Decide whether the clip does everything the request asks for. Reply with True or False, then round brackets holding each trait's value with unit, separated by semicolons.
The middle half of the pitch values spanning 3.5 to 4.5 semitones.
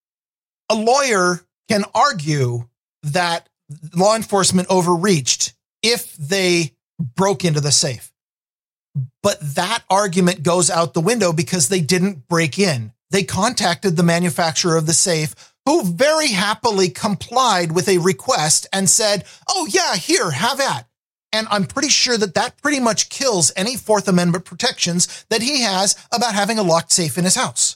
True (4.1 semitones)